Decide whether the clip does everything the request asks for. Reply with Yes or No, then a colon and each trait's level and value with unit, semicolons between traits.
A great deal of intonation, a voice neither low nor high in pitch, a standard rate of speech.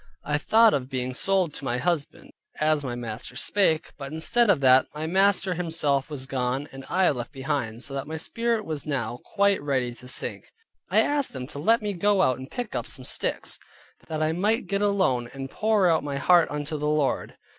No: wide, 6.3 semitones; medium, 150 Hz; fast, 210 wpm